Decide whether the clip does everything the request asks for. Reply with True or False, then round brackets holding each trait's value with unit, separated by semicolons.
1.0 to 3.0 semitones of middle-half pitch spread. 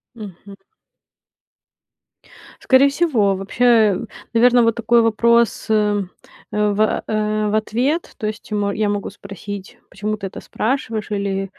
True (2.4 semitones)